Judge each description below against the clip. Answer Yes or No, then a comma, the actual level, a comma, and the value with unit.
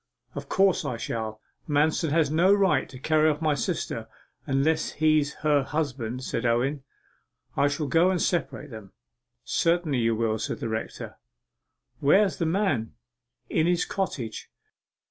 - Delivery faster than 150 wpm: No, average, 145 wpm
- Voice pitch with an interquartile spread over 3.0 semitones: Yes, average, 4.5 semitones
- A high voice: No, medium, 150 Hz